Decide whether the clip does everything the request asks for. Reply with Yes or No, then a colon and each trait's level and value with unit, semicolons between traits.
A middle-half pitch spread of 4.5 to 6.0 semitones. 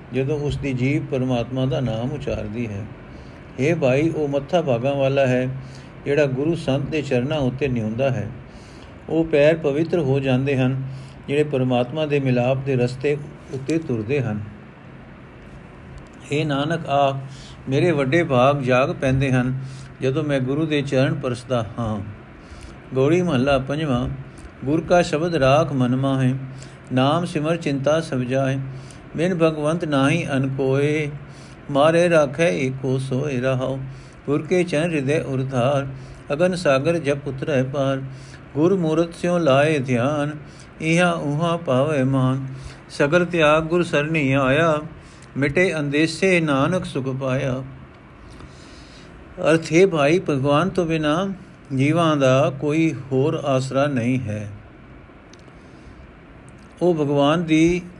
No: average, 2.9 semitones